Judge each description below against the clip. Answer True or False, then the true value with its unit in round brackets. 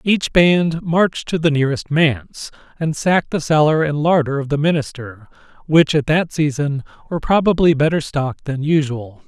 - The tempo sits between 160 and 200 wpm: True (170 wpm)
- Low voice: False (155 Hz)